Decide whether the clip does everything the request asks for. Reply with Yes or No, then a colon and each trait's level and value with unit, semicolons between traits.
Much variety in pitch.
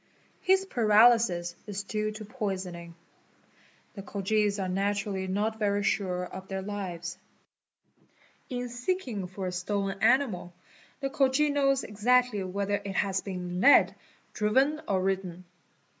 No: average, 3.9 semitones